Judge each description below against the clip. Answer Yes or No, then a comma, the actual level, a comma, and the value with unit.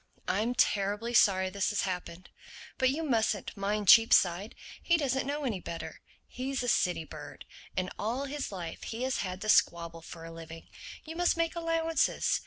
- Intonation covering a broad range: Yes, wide, 6.6 semitones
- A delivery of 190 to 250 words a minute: No, average, 175 wpm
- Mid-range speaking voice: No, high, 215 Hz